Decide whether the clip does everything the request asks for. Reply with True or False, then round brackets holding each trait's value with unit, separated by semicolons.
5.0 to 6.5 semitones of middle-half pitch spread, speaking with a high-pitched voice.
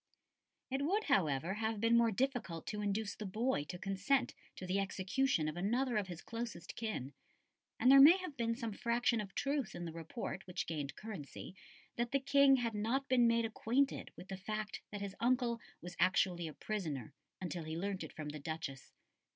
True (5.4 semitones; 215 Hz)